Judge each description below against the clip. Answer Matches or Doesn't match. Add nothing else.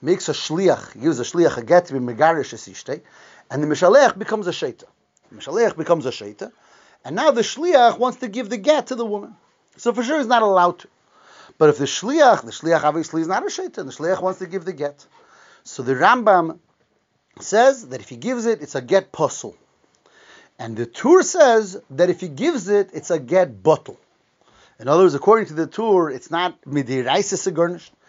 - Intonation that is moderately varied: Doesn't match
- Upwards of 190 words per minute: Matches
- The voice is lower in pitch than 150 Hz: Doesn't match